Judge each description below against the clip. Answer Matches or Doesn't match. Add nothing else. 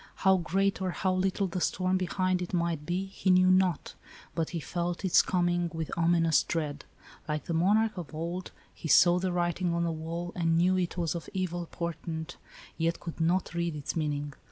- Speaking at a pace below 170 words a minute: Doesn't match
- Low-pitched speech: Doesn't match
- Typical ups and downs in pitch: Doesn't match